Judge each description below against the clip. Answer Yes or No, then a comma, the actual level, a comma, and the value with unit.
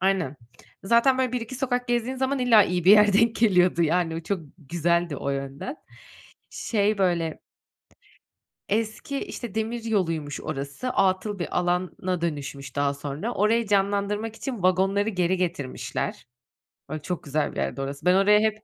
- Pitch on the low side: No, high, 190 Hz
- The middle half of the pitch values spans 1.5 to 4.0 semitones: No, average, 5.2 semitones